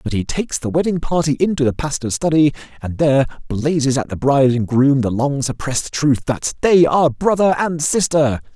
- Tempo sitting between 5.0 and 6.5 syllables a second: Yes, 5.5 syllables/s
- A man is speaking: Yes, male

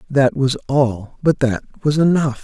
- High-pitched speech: No, low, 135 Hz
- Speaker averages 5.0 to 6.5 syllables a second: No, 4.1 syllables/s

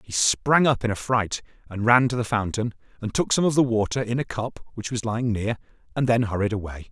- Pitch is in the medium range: No, low, 115 Hz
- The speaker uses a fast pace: Yes, fast, 245 wpm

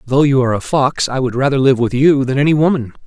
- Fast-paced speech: Yes, fast, 275 wpm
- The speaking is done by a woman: No, male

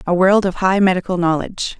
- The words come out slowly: No, average, 200 wpm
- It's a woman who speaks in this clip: Yes, female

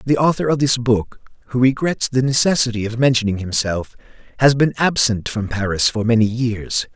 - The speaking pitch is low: Yes, low, 120 Hz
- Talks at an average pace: Yes, average, 175 wpm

